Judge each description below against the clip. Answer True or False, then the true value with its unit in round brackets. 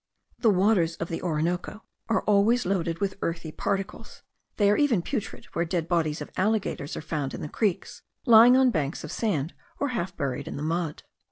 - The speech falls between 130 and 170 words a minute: False (190 wpm)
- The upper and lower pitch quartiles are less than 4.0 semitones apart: False (4.7 semitones)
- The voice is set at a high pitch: False (180 Hz)